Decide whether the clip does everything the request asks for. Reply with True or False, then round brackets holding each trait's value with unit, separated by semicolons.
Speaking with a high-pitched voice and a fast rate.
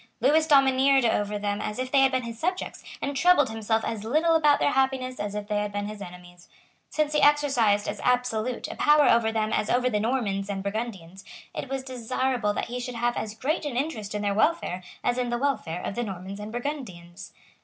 True (235 Hz; 220 wpm)